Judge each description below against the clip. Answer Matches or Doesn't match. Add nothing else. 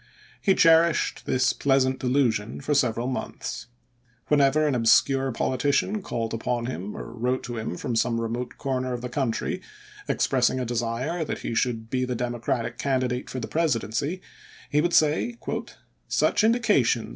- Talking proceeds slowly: Doesn't match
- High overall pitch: Doesn't match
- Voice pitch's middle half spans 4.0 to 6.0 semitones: Doesn't match